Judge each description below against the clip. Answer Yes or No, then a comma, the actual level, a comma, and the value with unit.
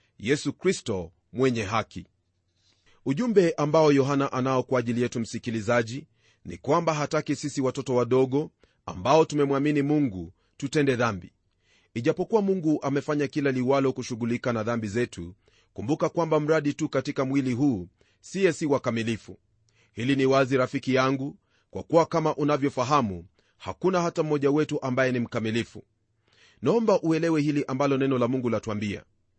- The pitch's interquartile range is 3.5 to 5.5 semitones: Yes, average, 4.8 semitones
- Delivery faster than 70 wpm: Yes, average, 135 wpm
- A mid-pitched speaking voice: No, low, 130 Hz